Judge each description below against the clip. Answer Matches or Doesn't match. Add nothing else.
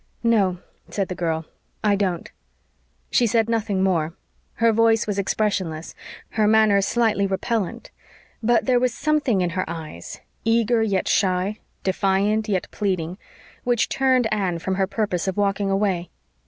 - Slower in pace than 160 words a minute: Matches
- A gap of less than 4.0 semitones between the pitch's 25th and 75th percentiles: Matches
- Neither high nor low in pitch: Doesn't match